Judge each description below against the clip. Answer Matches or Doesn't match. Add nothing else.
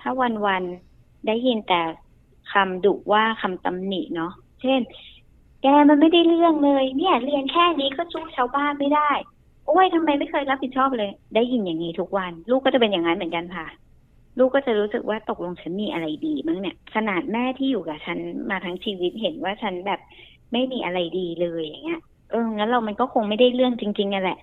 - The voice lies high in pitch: Matches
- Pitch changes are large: Matches